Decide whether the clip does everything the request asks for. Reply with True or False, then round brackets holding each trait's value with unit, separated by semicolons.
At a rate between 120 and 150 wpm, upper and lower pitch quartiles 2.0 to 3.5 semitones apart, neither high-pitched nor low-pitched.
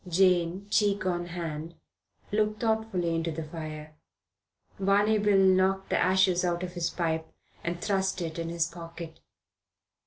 True (145 wpm; 2.5 semitones; 175 Hz)